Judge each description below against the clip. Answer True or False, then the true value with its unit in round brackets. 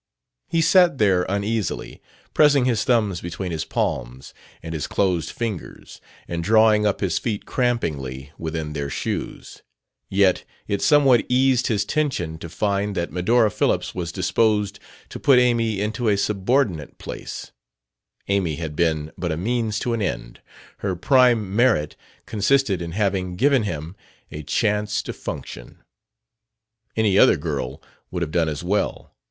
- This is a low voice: True (100 Hz)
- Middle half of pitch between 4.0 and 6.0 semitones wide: True (5.5 semitones)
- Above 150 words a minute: False (145 wpm)